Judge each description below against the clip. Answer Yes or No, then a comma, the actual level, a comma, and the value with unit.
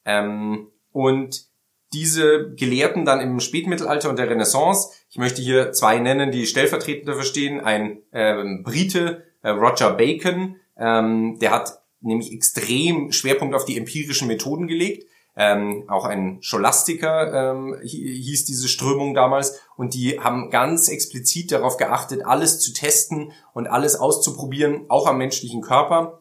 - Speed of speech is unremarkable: Yes, average, 140 wpm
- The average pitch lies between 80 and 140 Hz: Yes, low, 135 Hz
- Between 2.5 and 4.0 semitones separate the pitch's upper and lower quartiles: No, average, 4.8 semitones